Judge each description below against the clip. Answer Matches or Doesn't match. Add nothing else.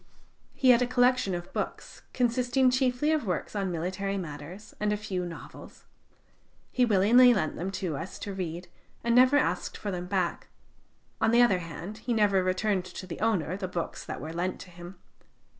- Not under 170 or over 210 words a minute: Matches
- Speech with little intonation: Doesn't match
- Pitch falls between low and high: Doesn't match